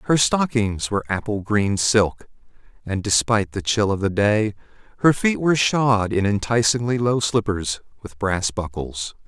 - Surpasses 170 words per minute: No, average, 155 wpm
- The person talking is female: No, male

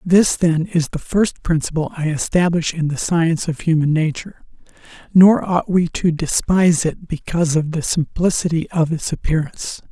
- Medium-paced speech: Yes, average, 165 wpm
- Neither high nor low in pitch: Yes, medium, 165 Hz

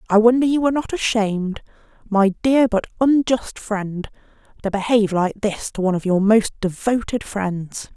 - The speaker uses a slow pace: No, average, 165 wpm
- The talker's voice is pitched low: No, high, 215 Hz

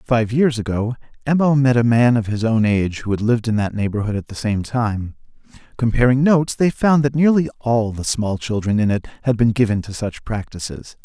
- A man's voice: Yes, male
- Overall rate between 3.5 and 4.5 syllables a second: No, 5.5 syllables/s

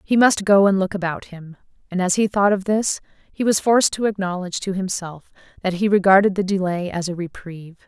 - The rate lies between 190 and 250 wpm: Yes, fast, 205 wpm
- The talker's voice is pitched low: No, high, 190 Hz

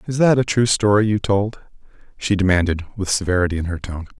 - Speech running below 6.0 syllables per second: No, 6.1 syllables/s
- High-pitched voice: No, low, 100 Hz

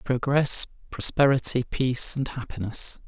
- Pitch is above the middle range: No, low, 130 Hz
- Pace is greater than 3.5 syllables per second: Yes, 4.6 syllables/s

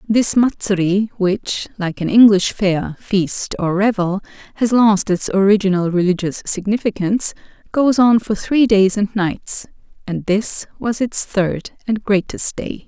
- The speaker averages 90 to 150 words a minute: Yes, average, 145 wpm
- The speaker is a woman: Yes, female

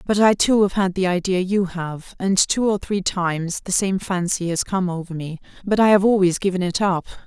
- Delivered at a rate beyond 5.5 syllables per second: No, 5.1 syllables/s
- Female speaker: Yes, female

